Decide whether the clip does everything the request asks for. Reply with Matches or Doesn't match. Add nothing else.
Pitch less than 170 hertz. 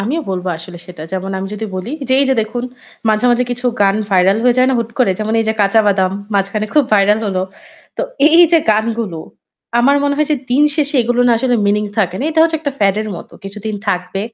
Doesn't match